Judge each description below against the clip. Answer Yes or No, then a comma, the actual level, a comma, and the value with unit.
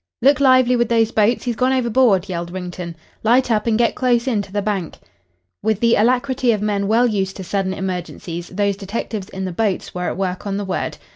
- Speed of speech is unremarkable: No, fast, 215 wpm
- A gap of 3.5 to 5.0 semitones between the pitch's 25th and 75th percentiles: Yes, average, 4.0 semitones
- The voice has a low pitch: No, high, 210 Hz